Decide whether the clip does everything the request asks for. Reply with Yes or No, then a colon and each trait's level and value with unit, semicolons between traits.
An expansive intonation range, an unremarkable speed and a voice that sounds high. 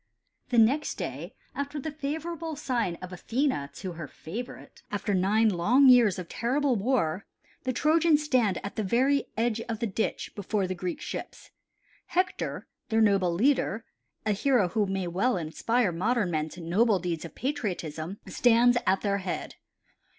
Yes: wide, 5.9 semitones; average, 160 wpm; high, 220 Hz